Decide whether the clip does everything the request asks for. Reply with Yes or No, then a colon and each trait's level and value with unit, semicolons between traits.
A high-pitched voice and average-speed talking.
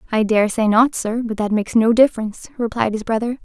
No: high, 225 Hz; fast, 225 wpm